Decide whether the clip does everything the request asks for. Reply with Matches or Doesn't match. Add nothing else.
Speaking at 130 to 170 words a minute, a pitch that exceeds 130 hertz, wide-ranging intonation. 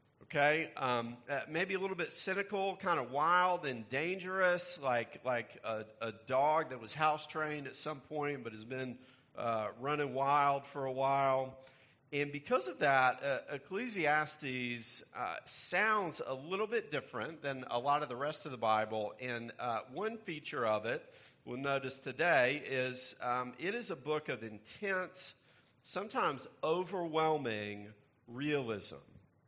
Doesn't match